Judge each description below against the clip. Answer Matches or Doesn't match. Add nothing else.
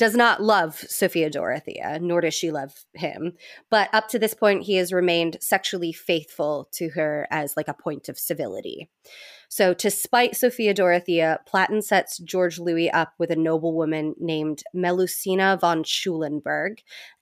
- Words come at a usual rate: Matches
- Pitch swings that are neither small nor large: Matches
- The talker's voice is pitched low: Doesn't match